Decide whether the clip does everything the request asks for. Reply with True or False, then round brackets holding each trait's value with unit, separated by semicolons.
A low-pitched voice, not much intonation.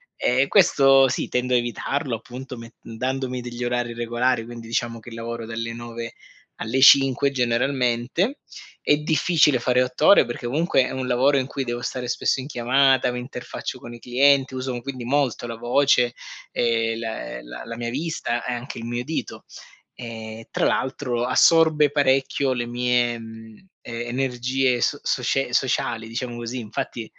True (125 Hz; 2.2 semitones)